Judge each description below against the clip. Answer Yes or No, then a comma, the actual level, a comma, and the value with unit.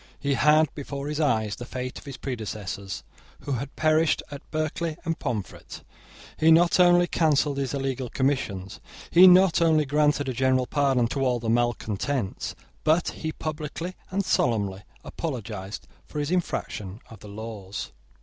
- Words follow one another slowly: No, average, 155 wpm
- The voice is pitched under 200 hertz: Yes, medium, 140 Hz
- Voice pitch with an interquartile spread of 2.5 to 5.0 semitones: No, wide, 5.4 semitones